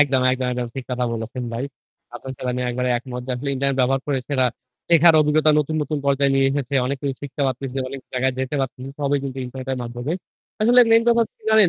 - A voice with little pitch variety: Yes, narrow, 2.3 semitones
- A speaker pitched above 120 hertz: Yes, low, 135 Hz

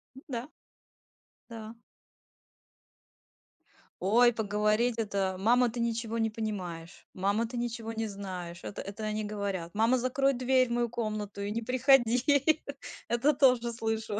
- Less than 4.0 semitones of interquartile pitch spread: Yes, average, 2.8 semitones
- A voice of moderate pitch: No, high, 225 Hz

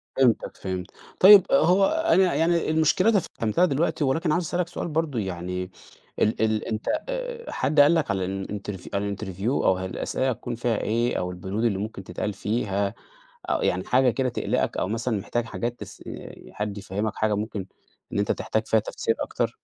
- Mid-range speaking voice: No, low, 115 Hz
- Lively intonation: Yes, wide, 7.7 semitones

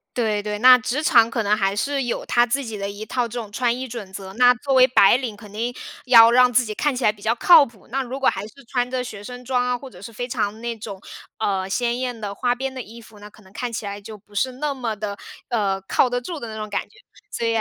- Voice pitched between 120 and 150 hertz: No, high, 235 Hz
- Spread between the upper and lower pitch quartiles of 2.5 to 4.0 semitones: Yes, average, 3.1 semitones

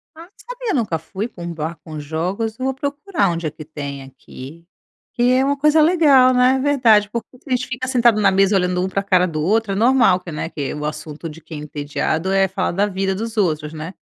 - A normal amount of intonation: No, wide, 7.8 semitones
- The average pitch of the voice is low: No, high, 195 Hz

